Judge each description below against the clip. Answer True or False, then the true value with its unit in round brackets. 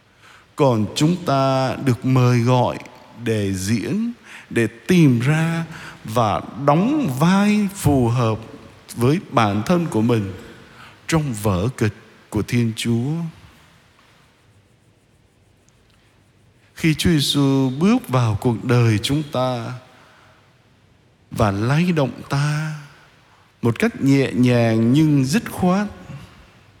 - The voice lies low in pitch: True (125 Hz)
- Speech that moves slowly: True (105 wpm)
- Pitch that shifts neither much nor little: True (4.6 semitones)